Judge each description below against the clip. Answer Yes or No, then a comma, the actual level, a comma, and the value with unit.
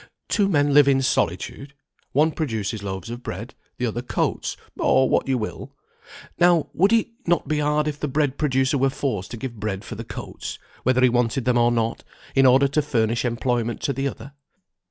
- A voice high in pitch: No, low, 130 Hz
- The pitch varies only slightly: No, average, 3.7 semitones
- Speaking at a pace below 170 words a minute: No, average, 195 wpm